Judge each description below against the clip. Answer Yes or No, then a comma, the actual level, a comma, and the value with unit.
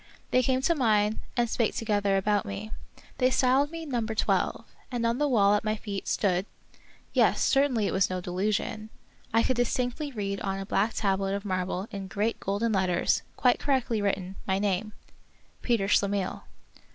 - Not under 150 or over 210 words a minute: Yes, average, 185 wpm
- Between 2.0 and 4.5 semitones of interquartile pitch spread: Yes, average, 3.5 semitones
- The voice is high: Yes, high, 210 Hz